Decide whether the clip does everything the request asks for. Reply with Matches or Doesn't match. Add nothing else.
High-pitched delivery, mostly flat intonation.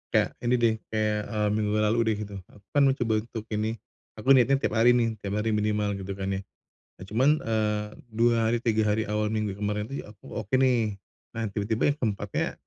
Doesn't match